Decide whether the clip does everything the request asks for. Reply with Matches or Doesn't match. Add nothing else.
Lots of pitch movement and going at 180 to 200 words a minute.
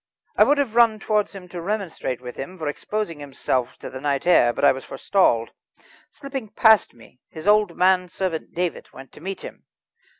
Matches